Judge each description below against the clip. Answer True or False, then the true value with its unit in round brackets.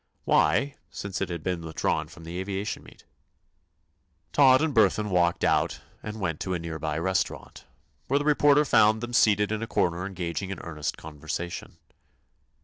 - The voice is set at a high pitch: False (95 Hz)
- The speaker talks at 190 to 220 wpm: False (165 wpm)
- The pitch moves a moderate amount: True (4.5 semitones)